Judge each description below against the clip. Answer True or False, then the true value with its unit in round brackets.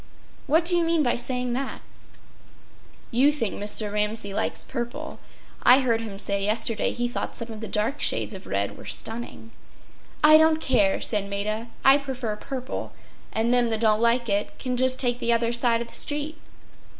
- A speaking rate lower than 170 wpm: False (185 wpm)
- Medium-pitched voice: False (235 Hz)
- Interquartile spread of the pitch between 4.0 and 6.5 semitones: False (3.3 semitones)